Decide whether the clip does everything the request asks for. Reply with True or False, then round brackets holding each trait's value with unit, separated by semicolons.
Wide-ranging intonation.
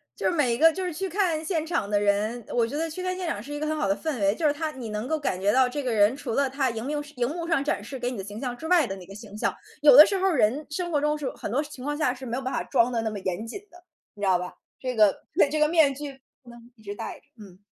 True (5.8 semitones)